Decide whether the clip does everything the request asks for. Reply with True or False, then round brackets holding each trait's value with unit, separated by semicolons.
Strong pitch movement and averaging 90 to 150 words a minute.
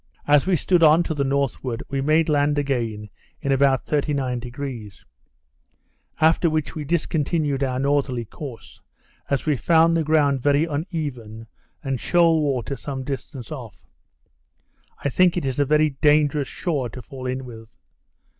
False (3.1 semitones; 145 wpm)